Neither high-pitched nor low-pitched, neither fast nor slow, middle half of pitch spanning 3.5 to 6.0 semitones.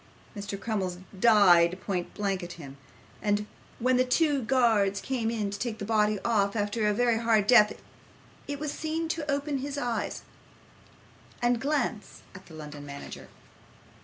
No: high, 220 Hz; average, 160 wpm; average, 4.1 semitones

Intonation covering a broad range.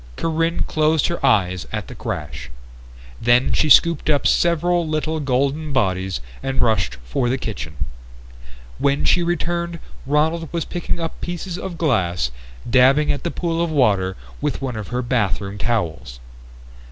Yes: wide, 8.0 semitones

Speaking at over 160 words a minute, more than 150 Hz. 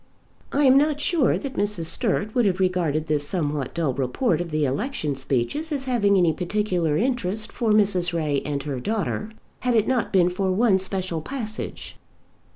Yes: average, 175 wpm; high, 190 Hz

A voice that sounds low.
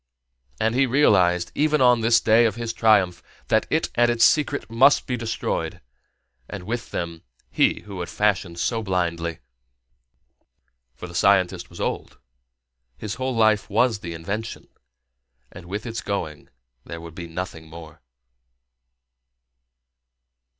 Yes: low, 105 Hz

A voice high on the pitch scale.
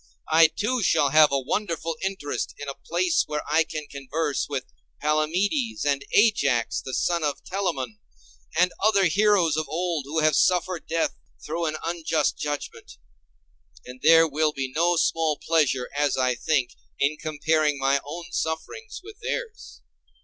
No: medium, 155 Hz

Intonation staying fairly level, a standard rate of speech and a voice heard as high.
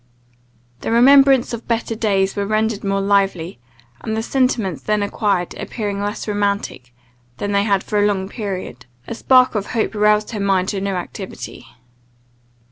Yes: narrow, 2.0 semitones; average, 160 wpm; high, 205 Hz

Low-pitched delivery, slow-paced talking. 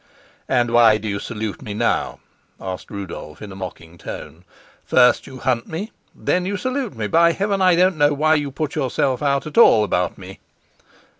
No: low, 130 Hz; average, 190 wpm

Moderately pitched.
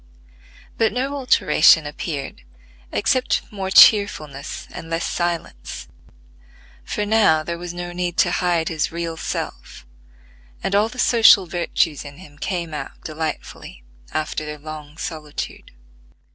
Yes: medium, 170 Hz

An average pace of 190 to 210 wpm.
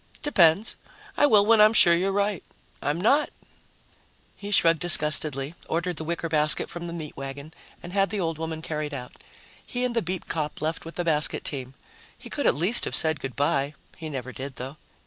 Yes: average, 200 wpm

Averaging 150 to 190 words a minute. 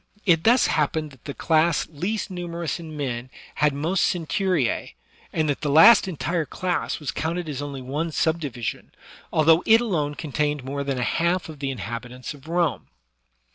Yes: average, 175 wpm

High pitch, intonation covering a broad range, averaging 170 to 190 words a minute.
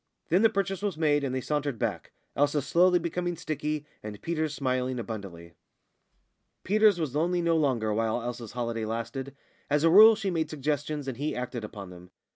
No: medium, 145 Hz; wide, 5.8 semitones; average, 180 wpm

